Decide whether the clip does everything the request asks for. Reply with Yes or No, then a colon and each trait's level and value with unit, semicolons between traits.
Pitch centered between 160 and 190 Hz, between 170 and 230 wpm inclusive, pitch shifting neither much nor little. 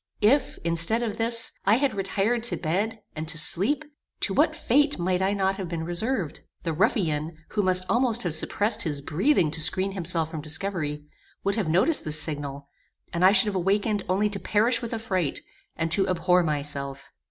Yes: medium, 185 Hz; average, 185 wpm; average, 4.9 semitones